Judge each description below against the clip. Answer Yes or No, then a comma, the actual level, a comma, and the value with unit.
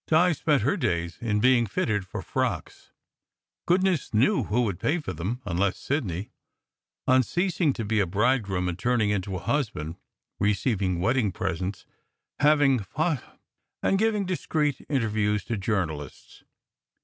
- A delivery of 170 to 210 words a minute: No, average, 150 wpm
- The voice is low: Yes, low, 110 Hz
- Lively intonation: Yes, wide, 7.2 semitones